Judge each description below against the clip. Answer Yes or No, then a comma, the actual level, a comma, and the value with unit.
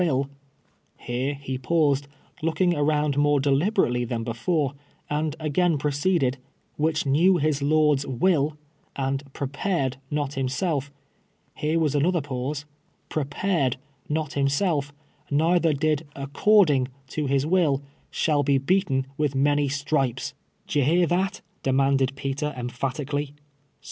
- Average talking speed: Yes, average, 145 wpm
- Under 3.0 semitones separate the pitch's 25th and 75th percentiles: Yes, narrow, 2.5 semitones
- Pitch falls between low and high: Yes, medium, 145 Hz